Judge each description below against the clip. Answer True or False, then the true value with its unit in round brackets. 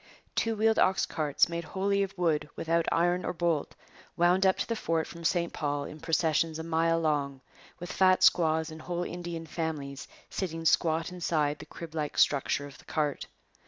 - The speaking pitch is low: False (165 Hz)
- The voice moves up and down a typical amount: False (2.2 semitones)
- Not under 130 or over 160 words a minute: False (185 wpm)